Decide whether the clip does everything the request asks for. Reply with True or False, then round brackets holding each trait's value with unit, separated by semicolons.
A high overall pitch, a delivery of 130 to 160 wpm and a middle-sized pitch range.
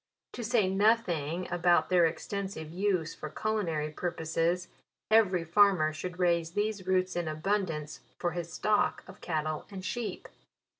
False (180 Hz; 145 wpm; 3.6 semitones)